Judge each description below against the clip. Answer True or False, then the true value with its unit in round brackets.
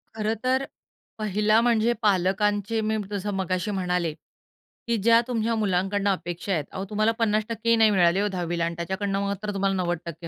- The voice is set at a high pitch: True (200 Hz)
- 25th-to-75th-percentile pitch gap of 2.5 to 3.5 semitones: True (2.8 semitones)